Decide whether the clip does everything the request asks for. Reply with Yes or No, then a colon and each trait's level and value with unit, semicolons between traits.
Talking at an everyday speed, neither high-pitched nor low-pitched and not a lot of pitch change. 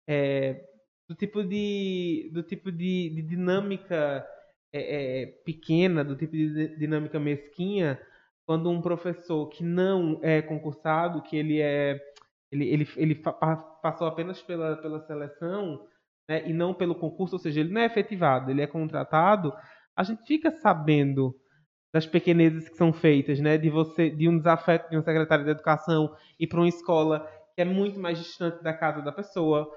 Yes: average, 170 wpm; medium, 160 Hz; narrow, 2.3 semitones